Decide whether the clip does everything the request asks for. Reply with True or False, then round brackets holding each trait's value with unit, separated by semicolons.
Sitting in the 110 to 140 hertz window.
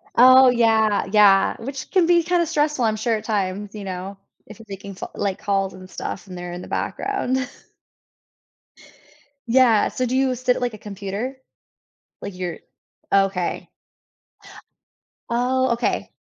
False (220 Hz)